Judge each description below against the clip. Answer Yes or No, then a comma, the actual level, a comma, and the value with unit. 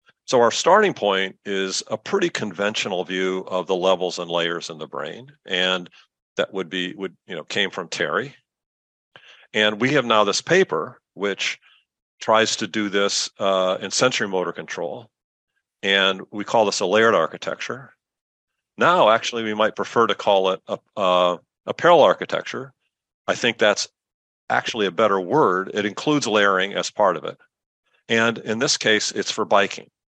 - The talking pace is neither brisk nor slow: Yes, average, 165 wpm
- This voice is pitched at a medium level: No, very low, 95 Hz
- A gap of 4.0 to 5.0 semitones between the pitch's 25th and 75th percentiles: No, average, 2.9 semitones